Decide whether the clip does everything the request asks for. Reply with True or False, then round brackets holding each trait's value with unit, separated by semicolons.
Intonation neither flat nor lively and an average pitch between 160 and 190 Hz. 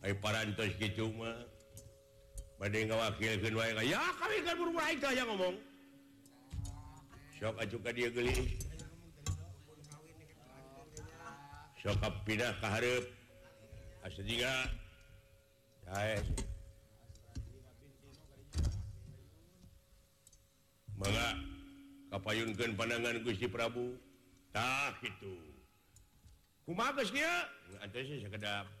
False (3.7 semitones; 110 Hz)